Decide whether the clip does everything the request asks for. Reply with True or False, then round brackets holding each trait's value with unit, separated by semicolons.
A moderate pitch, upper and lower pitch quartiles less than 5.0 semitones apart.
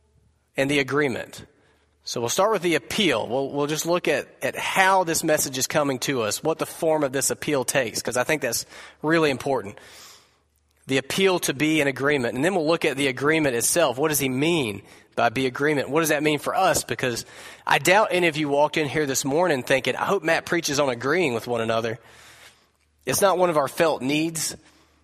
True (145 Hz; 4.6 semitones)